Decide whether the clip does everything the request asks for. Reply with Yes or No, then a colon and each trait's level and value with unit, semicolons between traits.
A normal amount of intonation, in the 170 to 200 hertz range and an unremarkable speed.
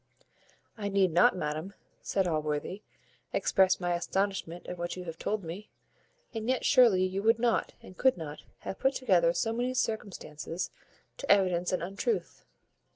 Yes: average, 3.9 semitones; medium, 185 Hz; average, 155 wpm